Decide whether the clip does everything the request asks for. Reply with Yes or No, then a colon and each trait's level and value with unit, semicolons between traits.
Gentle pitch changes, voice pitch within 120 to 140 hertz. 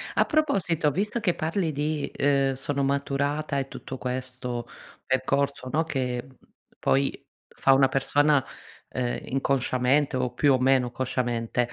Yes: narrow, 2.2 semitones; low, 135 Hz